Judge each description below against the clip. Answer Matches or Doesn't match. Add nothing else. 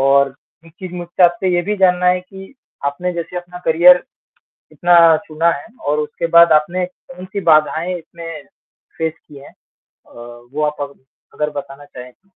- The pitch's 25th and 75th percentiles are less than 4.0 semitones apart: Matches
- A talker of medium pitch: Matches